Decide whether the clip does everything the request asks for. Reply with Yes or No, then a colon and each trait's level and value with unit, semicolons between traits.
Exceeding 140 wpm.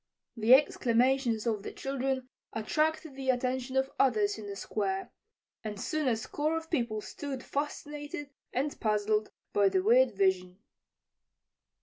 No: slow, 135 wpm